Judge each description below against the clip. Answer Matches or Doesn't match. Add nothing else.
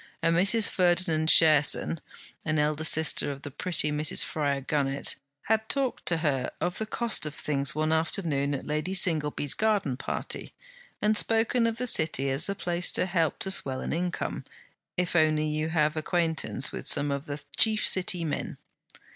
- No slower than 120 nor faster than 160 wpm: Doesn't match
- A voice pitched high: Doesn't match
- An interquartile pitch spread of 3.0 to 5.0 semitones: Matches